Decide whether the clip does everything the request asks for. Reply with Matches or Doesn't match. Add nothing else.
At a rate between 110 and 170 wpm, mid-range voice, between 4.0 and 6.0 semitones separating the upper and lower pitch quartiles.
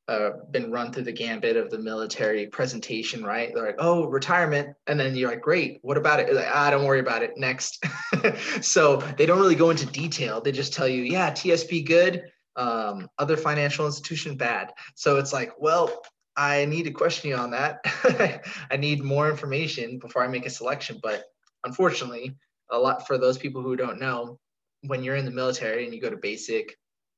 Doesn't match